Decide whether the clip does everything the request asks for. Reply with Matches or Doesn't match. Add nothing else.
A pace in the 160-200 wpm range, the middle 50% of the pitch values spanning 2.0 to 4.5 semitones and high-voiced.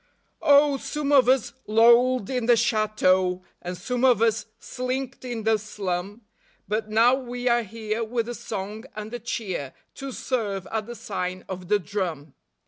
Matches